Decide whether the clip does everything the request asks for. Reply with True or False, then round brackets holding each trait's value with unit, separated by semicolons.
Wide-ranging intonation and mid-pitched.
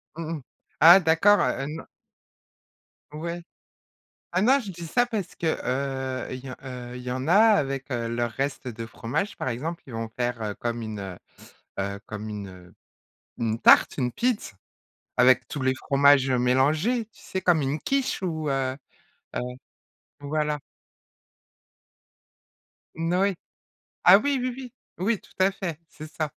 True (6.8 semitones; 145 Hz)